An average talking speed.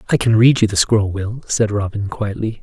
No: fast, 230 wpm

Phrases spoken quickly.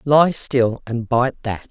No: average, 175 wpm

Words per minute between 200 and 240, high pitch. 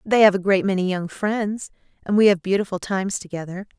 Yes: fast, 205 wpm; high, 195 Hz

